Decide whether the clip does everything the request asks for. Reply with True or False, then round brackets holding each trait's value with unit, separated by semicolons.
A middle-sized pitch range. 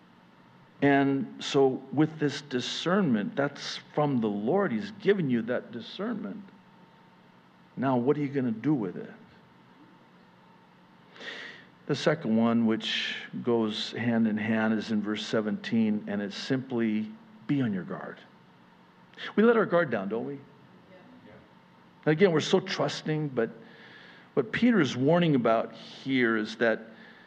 False (8.9 semitones)